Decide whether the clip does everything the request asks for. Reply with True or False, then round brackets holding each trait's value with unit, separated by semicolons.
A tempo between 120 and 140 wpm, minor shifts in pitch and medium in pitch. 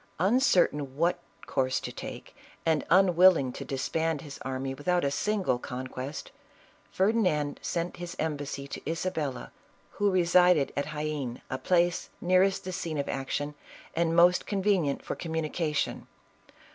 False (135 wpm; 4.2 semitones; 160 Hz)